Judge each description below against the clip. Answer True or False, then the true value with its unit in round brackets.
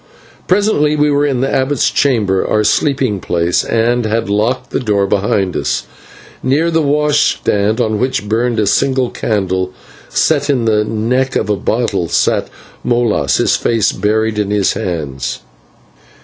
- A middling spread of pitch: True (4.6 semitones)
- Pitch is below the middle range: True (115 Hz)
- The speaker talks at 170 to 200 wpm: False (150 wpm)